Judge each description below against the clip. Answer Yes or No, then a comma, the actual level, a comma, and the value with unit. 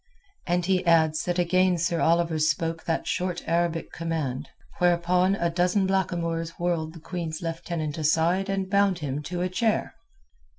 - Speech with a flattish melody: Yes, narrow, 1.8 semitones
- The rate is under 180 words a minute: Yes, average, 155 wpm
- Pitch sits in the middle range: Yes, medium, 170 Hz